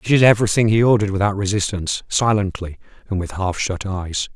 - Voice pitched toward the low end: Yes, low, 100 Hz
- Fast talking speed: No, average, 180 wpm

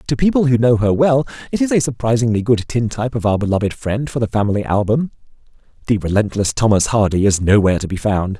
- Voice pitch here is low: Yes, low, 115 Hz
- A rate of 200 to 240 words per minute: Yes, fast, 205 wpm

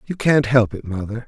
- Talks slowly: No, fast, 235 wpm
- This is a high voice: No, low, 120 Hz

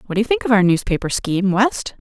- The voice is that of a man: No, female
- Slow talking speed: No, fast, 260 wpm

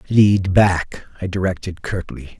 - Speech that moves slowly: Yes, slow, 125 wpm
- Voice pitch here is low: Yes, very low, 95 Hz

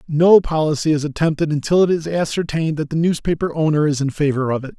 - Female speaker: No, male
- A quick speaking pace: Yes, fast, 215 wpm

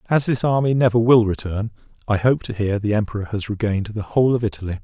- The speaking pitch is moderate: No, low, 110 Hz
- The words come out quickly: Yes, fast, 225 wpm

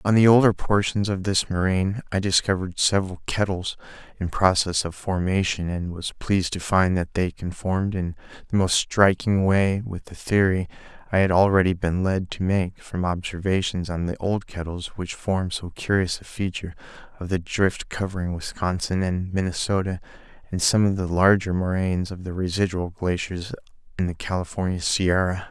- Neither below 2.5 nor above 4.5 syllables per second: No, 5.1 syllables/s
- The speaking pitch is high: No, very low, 95 Hz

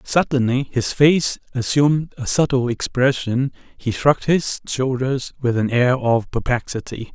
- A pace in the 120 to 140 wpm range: Yes, slow, 135 wpm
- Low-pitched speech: Yes, low, 130 Hz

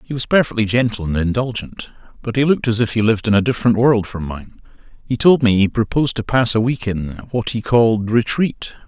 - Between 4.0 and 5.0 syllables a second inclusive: No, 6.0 syllables/s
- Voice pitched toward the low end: Yes, low, 115 Hz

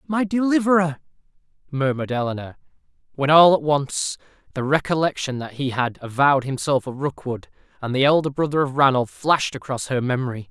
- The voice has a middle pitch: Yes, medium, 145 Hz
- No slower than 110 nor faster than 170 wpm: Yes, average, 155 wpm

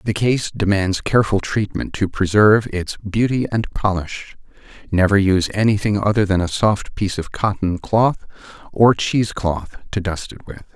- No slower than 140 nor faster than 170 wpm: Yes, average, 160 wpm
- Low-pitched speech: Yes, low, 100 Hz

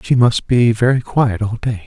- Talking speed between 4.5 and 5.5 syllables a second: Yes, 4.6 syllables/s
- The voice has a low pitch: Yes, low, 115 Hz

